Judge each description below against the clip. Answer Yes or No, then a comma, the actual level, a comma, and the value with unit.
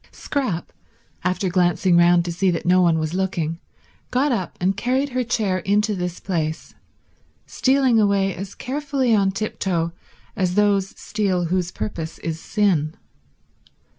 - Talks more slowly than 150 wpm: Yes, average, 140 wpm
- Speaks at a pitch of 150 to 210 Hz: Yes, high, 190 Hz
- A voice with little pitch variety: No, average, 3.4 semitones